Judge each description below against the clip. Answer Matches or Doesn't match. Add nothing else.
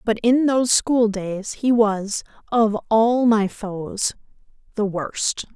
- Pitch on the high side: Matches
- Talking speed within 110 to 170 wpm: Matches